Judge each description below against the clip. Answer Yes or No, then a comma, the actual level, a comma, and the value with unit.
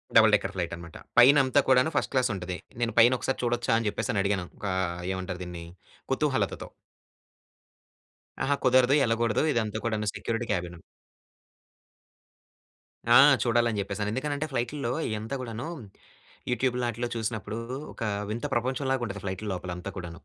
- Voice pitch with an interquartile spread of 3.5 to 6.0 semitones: Yes, average, 3.9 semitones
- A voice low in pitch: Yes, low, 115 Hz